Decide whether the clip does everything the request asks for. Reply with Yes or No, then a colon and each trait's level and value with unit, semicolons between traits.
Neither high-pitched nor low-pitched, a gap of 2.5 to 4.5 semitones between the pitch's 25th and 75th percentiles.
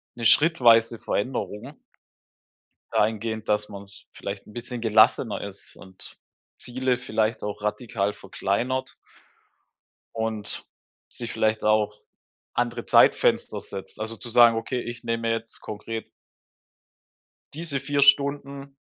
No: low, 115 Hz; average, 2.8 semitones